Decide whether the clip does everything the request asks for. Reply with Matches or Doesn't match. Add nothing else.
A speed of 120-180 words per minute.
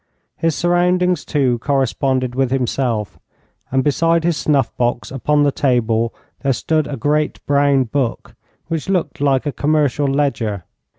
Matches